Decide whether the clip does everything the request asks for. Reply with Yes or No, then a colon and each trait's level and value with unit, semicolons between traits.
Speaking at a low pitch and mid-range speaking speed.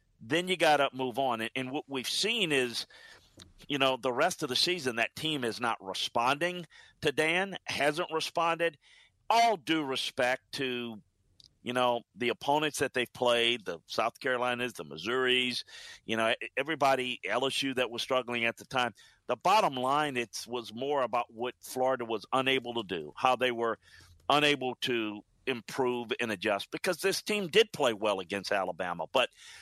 Yes: low, 130 Hz; average, 170 wpm